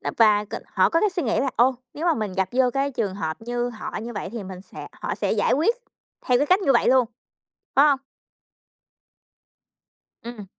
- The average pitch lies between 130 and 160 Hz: No, high, 245 Hz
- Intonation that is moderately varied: Yes, average, 4.7 semitones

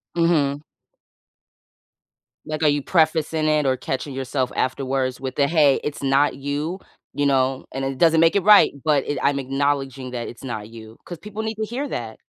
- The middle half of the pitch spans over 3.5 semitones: No, average, 3.1 semitones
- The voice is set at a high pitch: No, medium, 140 Hz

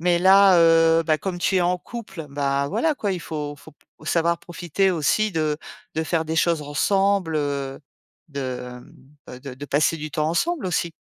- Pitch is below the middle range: No, medium, 165 Hz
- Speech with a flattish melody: No, average, 3.6 semitones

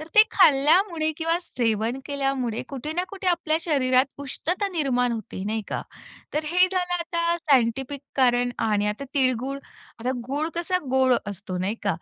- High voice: Yes, very high, 275 Hz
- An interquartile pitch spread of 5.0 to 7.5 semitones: Yes, wide, 5.5 semitones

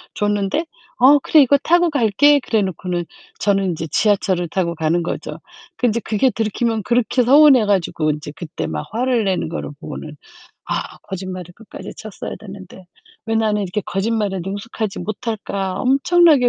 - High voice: Yes, high, 210 Hz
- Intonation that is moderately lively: Yes, average, 4.5 semitones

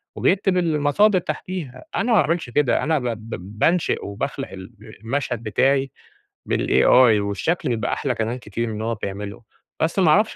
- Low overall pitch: Yes, low, 130 Hz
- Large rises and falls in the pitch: Yes, wide, 6.7 semitones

